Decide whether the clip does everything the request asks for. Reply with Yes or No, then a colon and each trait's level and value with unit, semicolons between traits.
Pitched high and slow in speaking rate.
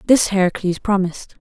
Yes: high, 195 Hz; slow, 125 wpm